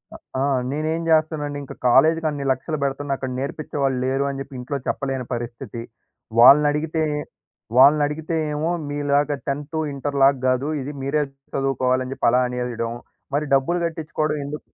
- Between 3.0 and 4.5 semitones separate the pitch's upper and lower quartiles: No, narrow, 2.4 semitones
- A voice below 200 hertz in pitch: Yes, medium, 140 Hz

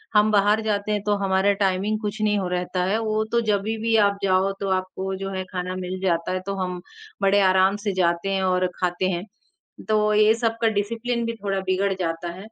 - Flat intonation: Yes, narrow, 2.3 semitones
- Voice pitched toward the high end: Yes, high, 195 Hz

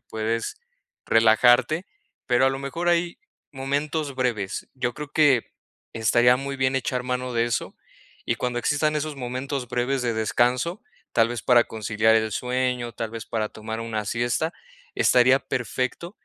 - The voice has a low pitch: Yes, low, 125 Hz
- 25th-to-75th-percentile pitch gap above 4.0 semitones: No, average, 3.1 semitones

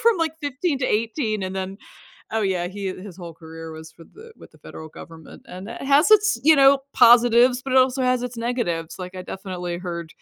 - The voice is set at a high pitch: Yes, high, 215 Hz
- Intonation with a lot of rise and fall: Yes, wide, 6.7 semitones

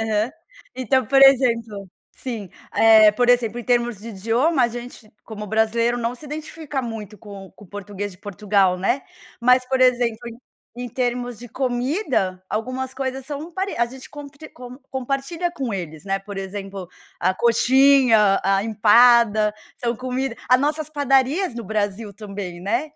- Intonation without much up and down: No, average, 4.0 semitones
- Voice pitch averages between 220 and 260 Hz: Yes, high, 235 Hz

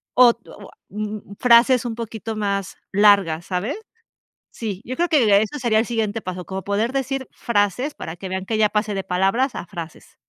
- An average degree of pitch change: Yes, average, 3.5 semitones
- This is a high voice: Yes, high, 215 Hz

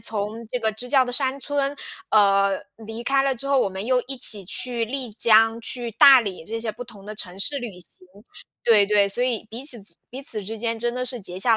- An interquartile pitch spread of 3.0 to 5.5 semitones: Yes, average, 3.3 semitones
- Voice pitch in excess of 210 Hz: Yes, high, 230 Hz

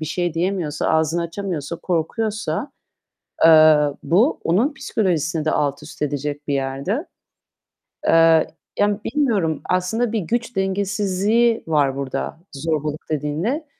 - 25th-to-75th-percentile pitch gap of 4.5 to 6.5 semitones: Yes, average, 5.3 semitones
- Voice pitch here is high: No, medium, 170 Hz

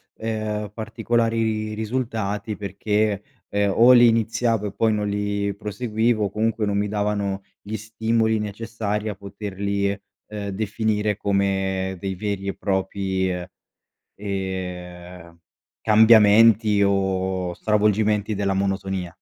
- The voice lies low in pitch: Yes, low, 105 Hz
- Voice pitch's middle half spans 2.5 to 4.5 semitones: No, narrow, 1.9 semitones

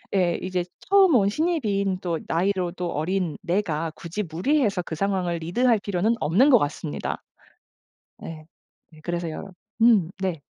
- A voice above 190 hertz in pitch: No, medium, 185 Hz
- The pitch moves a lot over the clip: No, average, 3.7 semitones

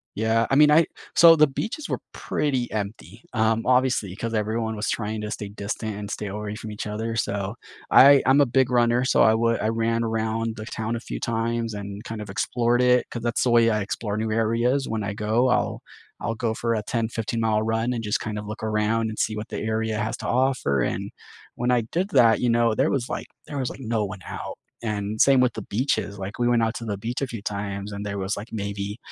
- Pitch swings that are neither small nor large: No, narrow, 2.1 semitones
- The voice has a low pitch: Yes, low, 110 Hz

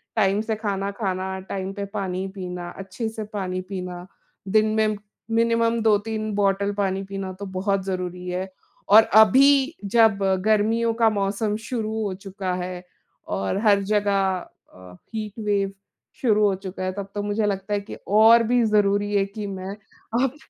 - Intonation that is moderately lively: No, narrow, 2.3 semitones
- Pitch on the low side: No, high, 200 Hz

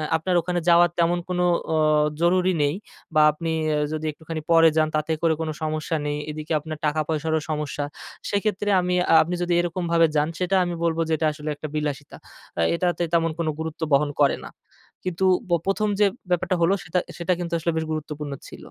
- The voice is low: No, medium, 165 Hz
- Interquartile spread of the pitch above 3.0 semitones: No, narrow, 2.4 semitones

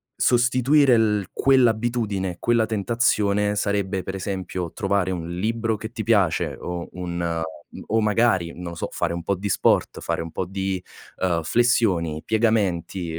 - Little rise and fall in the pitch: No, average, 4.1 semitones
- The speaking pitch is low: Yes, low, 100 Hz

